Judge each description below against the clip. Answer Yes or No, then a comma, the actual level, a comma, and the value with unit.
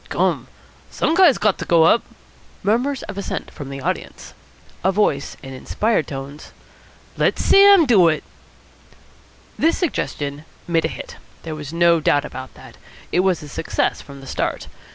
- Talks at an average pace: Yes, average, 160 wpm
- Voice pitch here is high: No, medium, 170 Hz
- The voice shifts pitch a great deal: Yes, wide, 6.9 semitones